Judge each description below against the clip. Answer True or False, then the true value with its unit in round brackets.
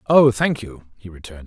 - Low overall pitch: True (110 Hz)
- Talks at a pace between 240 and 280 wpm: False (205 wpm)